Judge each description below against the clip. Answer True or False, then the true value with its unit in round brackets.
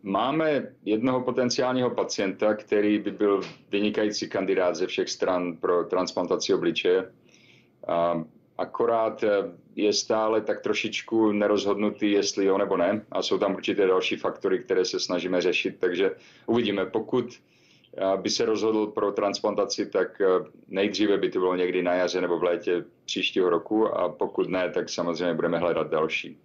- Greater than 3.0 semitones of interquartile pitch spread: True (4.2 semitones)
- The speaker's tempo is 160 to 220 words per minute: False (145 wpm)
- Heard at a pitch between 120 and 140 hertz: False (110 Hz)